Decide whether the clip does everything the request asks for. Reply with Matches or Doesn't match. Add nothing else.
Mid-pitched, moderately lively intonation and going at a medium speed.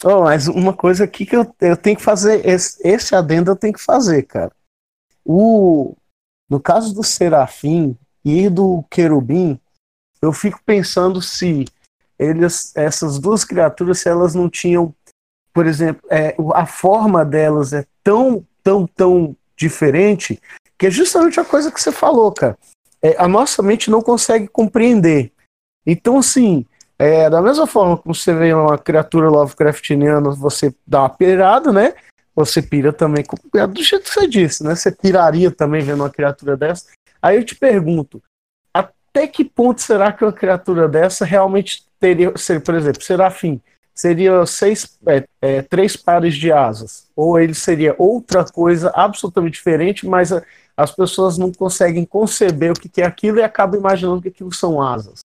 Matches